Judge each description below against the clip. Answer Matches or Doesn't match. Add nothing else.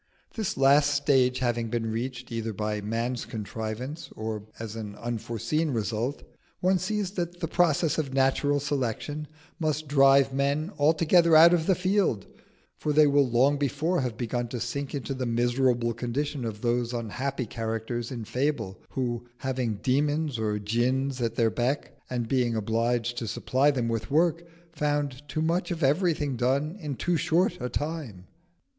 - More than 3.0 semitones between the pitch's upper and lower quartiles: Matches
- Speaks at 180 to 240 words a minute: Doesn't match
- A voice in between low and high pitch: Doesn't match